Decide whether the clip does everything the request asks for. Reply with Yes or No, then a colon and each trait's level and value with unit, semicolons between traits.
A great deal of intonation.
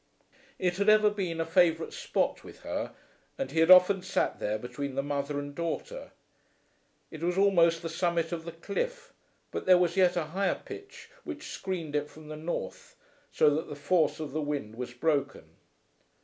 No: average, 4.1 semitones